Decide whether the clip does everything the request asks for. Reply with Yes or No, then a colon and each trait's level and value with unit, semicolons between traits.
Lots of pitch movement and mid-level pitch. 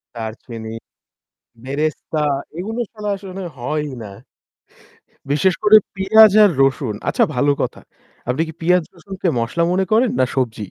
Yes: wide, 7.0 semitones; medium, 160 Hz